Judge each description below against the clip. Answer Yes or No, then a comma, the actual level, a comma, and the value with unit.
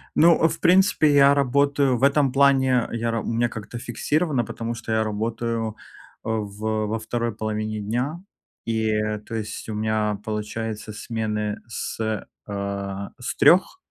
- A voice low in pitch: Yes, low, 115 Hz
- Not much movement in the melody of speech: No, average, 4.0 semitones